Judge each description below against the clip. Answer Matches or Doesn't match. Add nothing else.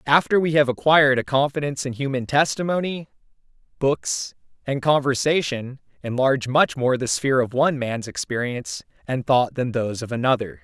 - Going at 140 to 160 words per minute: Matches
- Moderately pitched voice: Doesn't match